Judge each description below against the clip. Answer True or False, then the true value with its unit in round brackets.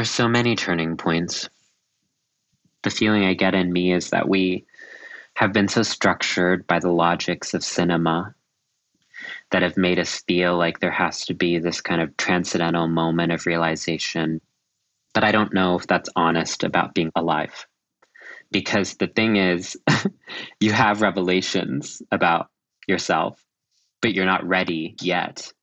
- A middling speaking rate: True (150 wpm)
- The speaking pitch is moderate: False (90 Hz)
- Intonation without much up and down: True (2.3 semitones)